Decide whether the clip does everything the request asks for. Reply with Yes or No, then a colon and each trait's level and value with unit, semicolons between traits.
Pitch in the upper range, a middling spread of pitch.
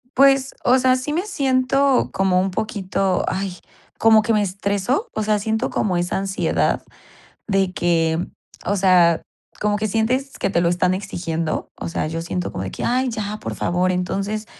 Yes: high, 200 Hz; average, 4.2 semitones